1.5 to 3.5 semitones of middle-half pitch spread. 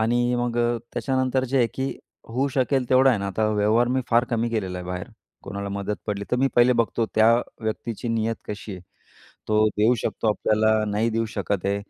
Yes: average, 2.7 semitones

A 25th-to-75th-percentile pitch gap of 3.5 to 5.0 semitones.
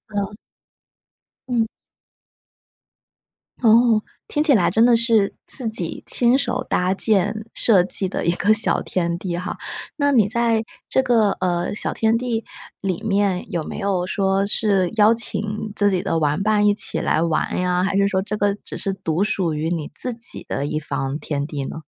Yes: average, 3.8 semitones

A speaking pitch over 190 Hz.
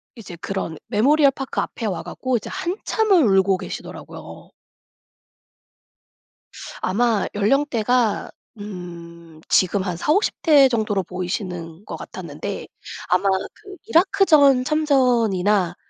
Yes: high, 215 Hz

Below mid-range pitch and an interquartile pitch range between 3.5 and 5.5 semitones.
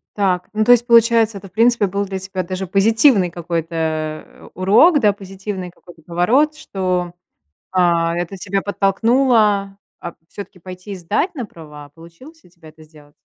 No: high, 190 Hz; average, 3.9 semitones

